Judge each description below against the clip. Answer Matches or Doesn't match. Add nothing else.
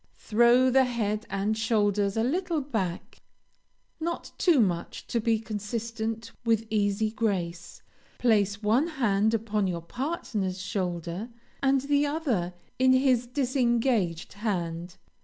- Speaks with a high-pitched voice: Matches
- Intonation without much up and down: Doesn't match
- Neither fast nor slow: Doesn't match